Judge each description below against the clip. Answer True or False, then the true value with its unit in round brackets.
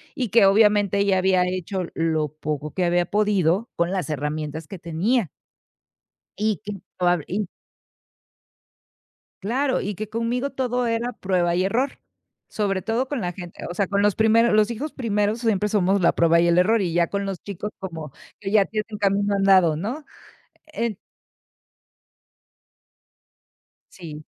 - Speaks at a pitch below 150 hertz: False (200 Hz)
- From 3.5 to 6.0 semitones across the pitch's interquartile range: True (3.9 semitones)